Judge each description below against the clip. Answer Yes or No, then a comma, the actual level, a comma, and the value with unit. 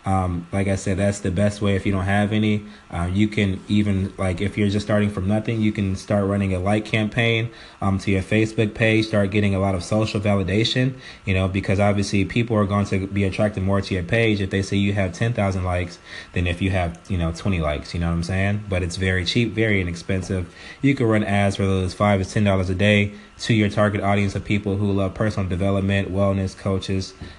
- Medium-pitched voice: No, low, 100 Hz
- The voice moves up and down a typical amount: No, narrow, 1.7 semitones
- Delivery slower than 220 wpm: No, fast, 235 wpm